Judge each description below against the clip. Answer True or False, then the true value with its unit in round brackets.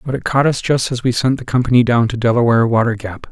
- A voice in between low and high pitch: False (120 Hz)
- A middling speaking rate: False (270 wpm)